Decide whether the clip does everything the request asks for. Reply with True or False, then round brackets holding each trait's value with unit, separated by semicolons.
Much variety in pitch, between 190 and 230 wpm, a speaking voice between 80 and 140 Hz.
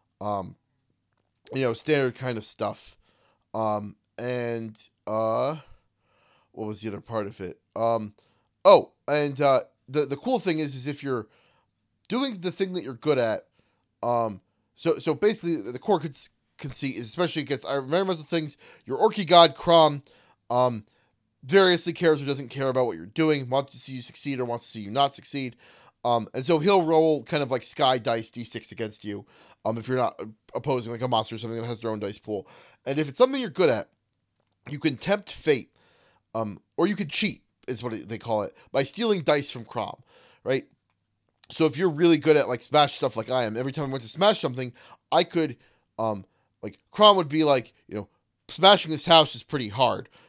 True (5.7 semitones; 200 wpm; 135 Hz)